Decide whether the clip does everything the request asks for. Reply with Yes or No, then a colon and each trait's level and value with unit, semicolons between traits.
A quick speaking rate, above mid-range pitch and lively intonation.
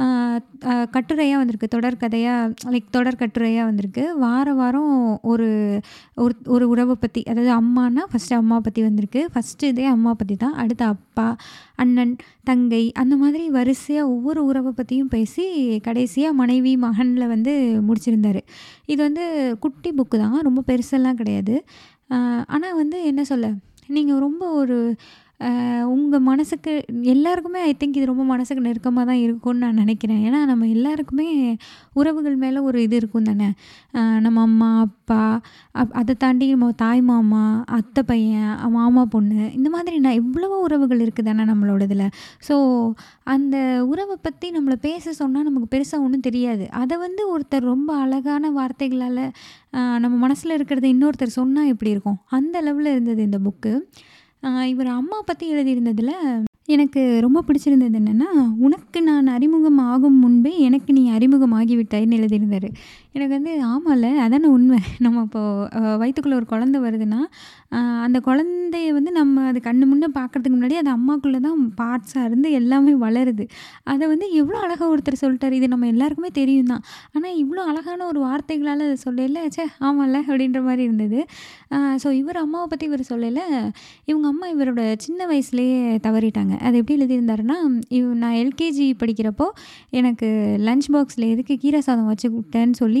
No: fast, 145 wpm; very high, 255 Hz; average, 3.4 semitones